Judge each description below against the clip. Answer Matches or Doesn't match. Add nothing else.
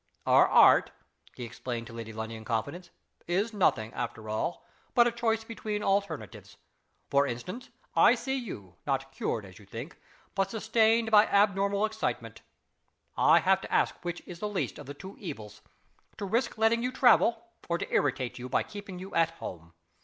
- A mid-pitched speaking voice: Matches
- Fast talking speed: Doesn't match